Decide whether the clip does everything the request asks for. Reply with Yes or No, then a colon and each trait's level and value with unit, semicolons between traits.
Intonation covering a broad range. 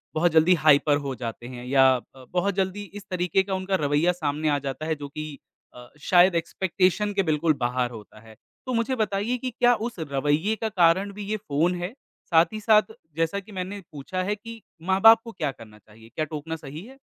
Yes: wide, 5.7 semitones